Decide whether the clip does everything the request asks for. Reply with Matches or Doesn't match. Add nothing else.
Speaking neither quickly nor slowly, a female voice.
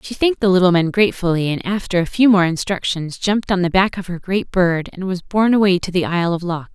Doesn't match